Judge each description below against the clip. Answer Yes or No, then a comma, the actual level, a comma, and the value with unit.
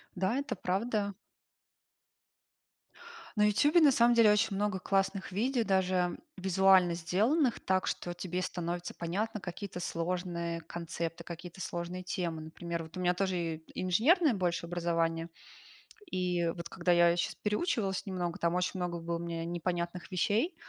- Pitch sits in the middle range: Yes, medium, 180 Hz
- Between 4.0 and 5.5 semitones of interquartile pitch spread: No, average, 2.7 semitones